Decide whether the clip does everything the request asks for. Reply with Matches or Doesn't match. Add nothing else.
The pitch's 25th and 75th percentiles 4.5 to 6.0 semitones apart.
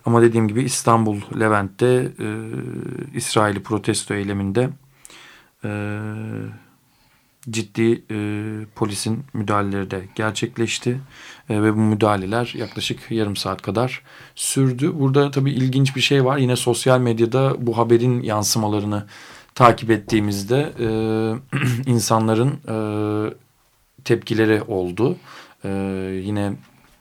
Doesn't match